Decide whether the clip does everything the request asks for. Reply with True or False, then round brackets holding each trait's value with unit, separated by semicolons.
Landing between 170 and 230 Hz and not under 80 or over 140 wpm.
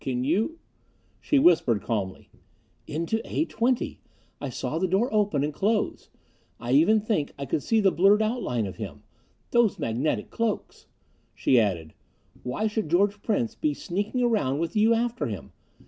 False (190 Hz; 165 wpm)